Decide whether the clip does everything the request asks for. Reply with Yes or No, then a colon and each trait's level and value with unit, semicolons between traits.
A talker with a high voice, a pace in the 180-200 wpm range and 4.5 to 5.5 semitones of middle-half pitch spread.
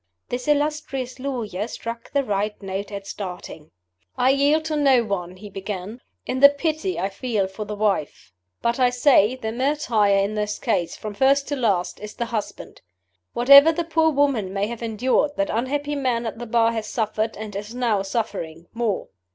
Yes: high, 230 Hz; average, 185 wpm; average, 4.9 semitones